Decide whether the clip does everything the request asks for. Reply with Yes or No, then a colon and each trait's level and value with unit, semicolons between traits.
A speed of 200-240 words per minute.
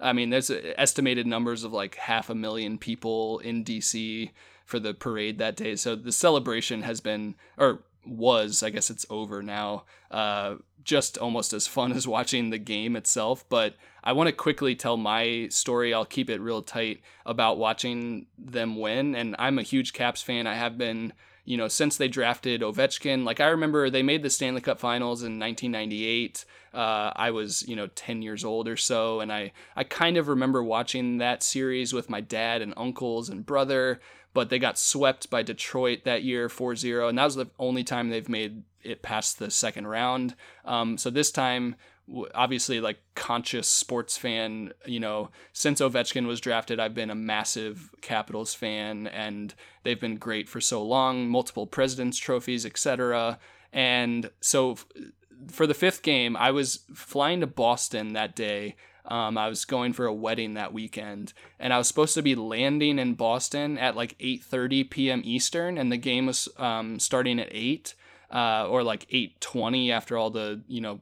No: average, 185 wpm